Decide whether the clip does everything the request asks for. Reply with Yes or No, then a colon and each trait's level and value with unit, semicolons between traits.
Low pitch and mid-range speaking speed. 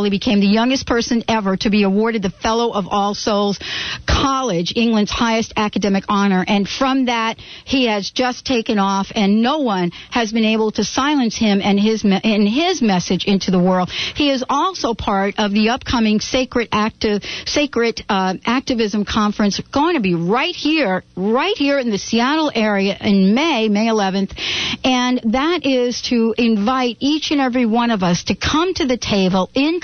No: high, 225 Hz; average, 180 wpm